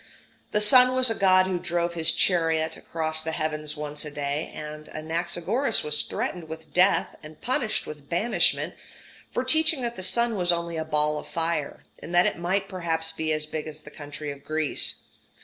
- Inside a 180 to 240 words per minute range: Yes, average, 190 wpm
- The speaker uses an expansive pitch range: No, average, 3.3 semitones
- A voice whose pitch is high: No, medium, 165 Hz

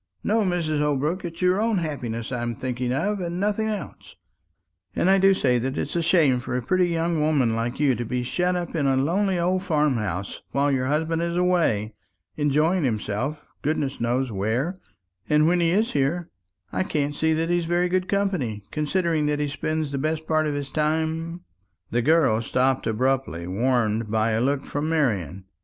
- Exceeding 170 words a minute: Yes, average, 190 wpm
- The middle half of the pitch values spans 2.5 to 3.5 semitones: No, wide, 5.4 semitones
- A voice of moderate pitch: Yes, medium, 150 Hz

